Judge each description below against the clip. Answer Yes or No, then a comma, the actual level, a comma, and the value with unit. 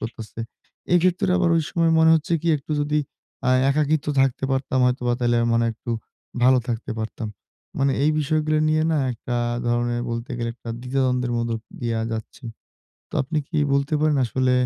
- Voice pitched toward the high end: No, low, 130 Hz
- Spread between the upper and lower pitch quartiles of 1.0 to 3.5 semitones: No, average, 4.4 semitones